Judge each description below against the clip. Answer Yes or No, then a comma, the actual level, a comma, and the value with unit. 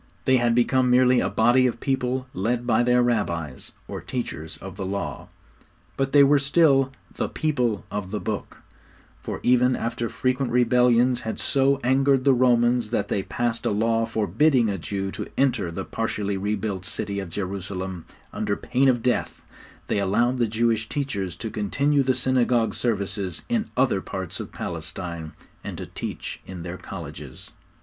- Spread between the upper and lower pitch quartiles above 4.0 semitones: Yes, average, 4.4 semitones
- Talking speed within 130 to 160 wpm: No, average, 170 wpm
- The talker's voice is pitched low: Yes, low, 115 Hz